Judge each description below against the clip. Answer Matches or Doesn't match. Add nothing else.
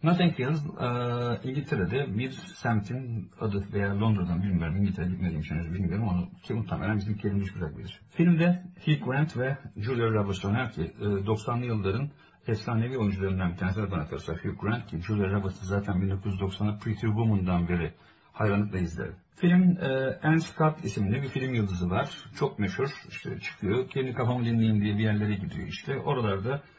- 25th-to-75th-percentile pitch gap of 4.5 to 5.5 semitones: Matches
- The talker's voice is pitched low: Matches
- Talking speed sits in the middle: Matches